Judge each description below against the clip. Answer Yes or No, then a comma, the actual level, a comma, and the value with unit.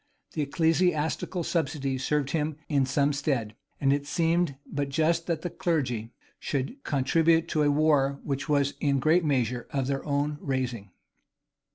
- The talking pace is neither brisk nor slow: Yes, average, 160 wpm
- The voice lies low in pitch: No, medium, 145 Hz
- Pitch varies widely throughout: No, average, 2.8 semitones